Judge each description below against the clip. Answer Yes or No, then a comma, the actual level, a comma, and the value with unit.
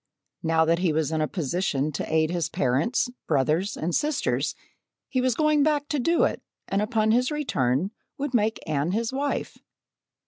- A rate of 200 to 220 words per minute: No, average, 175 wpm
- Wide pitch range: Yes, wide, 8.5 semitones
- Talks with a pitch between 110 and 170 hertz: No, high, 190 Hz